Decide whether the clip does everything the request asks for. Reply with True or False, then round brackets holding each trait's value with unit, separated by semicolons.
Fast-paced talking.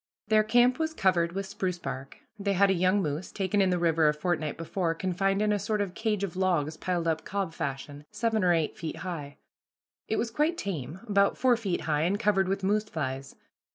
True (215 wpm)